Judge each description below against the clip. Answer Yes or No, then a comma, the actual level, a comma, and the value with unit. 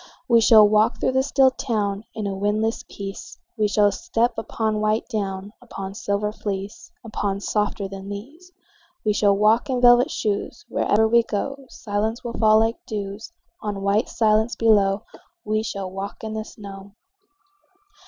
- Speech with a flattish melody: Yes, narrow, 2.2 semitones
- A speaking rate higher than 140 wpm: Yes, average, 160 wpm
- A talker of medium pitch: No, high, 215 Hz